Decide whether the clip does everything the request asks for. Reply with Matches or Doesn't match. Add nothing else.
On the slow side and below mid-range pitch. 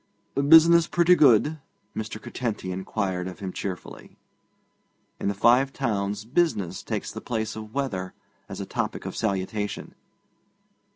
Matches